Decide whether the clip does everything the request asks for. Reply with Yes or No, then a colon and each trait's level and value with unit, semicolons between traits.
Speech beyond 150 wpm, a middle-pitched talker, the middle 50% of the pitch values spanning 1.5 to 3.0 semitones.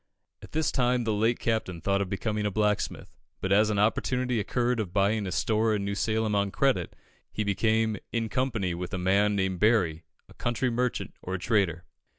No: average, 190 wpm; low, 105 Hz; average, 2.7 semitones